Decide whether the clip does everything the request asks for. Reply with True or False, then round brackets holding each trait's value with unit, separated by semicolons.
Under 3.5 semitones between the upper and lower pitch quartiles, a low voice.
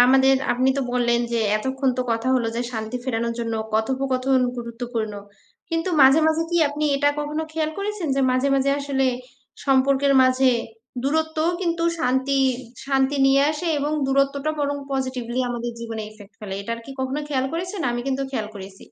False (3.0 semitones; 265 Hz)